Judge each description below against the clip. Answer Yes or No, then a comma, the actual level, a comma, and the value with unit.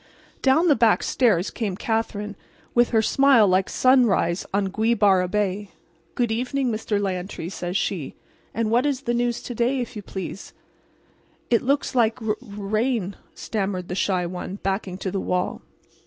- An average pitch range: Yes, average, 3.9 semitones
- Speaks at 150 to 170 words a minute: Yes, average, 160 wpm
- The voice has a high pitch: Yes, high, 215 Hz